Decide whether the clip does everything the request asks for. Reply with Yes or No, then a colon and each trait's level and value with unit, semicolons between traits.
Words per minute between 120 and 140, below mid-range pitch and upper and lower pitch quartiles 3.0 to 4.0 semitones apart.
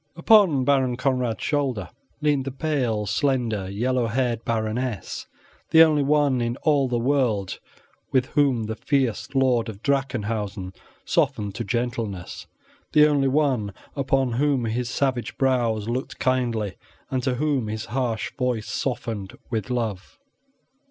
Yes: slow, 135 wpm; low, 125 Hz; average, 3.5 semitones